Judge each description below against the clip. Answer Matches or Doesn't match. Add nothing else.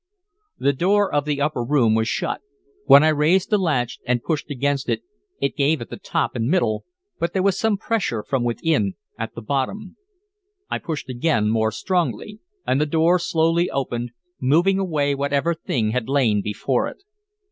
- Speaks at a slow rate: Doesn't match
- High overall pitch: Doesn't match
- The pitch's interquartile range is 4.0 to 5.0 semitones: Doesn't match